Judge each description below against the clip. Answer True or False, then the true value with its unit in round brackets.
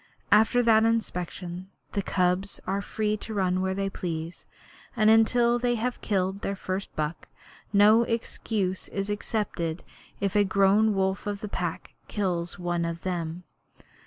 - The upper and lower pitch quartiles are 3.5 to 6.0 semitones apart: False (3.0 semitones)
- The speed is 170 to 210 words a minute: False (150 wpm)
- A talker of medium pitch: False (195 Hz)